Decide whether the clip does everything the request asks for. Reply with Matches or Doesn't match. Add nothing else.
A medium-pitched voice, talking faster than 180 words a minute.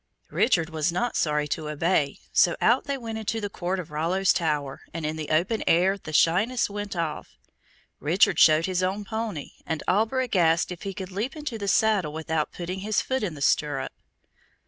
Matches